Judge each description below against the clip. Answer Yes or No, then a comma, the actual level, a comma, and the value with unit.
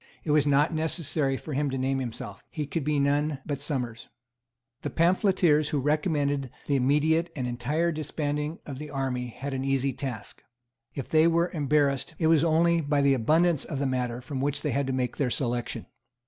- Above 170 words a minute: Yes, average, 190 wpm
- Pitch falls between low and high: Yes, medium, 145 Hz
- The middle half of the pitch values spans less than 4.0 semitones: Yes, average, 2.7 semitones